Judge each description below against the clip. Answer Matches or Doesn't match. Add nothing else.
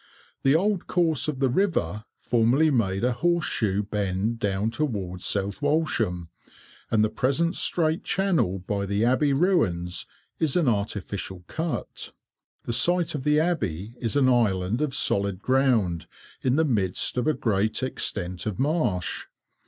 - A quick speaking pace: Doesn't match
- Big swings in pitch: Matches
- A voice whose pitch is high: Doesn't match